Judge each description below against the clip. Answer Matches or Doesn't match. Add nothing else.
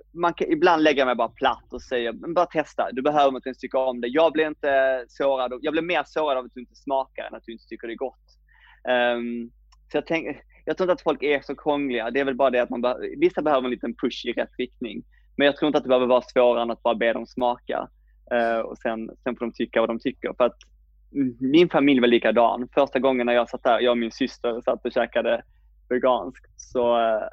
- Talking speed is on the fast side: Matches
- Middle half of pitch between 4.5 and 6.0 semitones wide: Doesn't match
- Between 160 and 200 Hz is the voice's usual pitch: Doesn't match